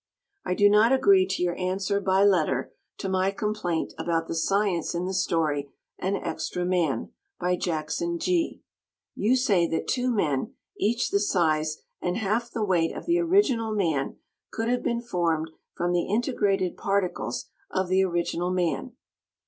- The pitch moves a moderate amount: Yes, average, 4.1 semitones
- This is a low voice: No, high, 190 Hz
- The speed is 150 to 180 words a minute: Yes, average, 160 wpm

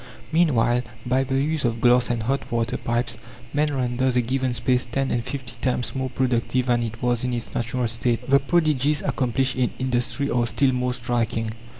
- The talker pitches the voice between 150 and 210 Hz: No, low, 125 Hz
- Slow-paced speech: No, average, 190 wpm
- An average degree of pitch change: No, narrow, 1.9 semitones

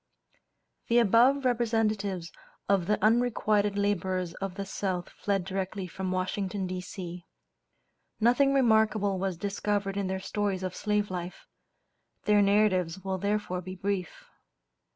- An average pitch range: No, narrow, 2.3 semitones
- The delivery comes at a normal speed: No, slow, 125 wpm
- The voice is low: No, high, 200 Hz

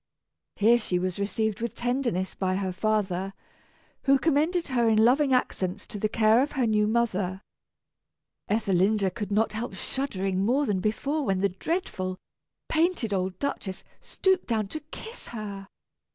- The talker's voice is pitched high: Yes, high, 215 Hz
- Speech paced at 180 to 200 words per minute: No, average, 150 wpm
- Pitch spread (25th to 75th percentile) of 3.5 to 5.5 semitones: Yes, average, 5.1 semitones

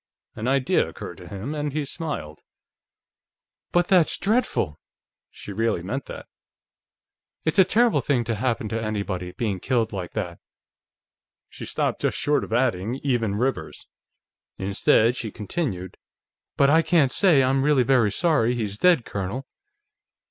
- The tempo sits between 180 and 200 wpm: No, average, 145 wpm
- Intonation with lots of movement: Yes, wide, 6.1 semitones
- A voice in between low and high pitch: No, low, 120 Hz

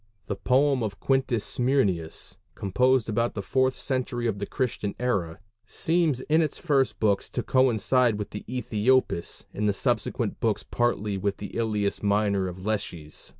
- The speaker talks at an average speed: Yes, average, 150 wpm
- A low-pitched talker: Yes, low, 115 Hz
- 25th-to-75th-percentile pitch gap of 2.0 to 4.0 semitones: No, average, 4.4 semitones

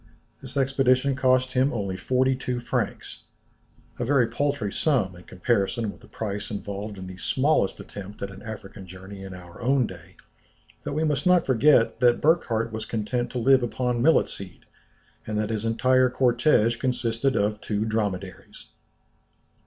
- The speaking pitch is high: No, low, 115 Hz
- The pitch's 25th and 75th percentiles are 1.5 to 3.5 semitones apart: No, average, 4.2 semitones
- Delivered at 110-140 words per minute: No, average, 160 wpm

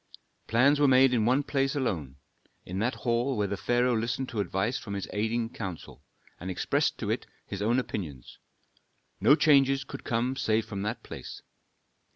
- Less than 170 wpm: No, average, 175 wpm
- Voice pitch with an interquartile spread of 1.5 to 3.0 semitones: No, average, 4.5 semitones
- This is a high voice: No, low, 115 Hz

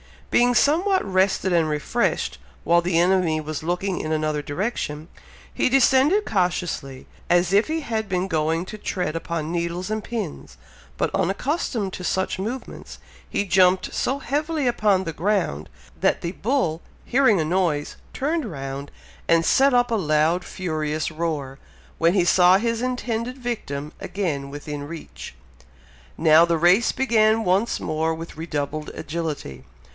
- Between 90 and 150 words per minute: Yes, average, 145 wpm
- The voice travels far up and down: Yes, wide, 6.1 semitones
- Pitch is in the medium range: Yes, medium, 180 Hz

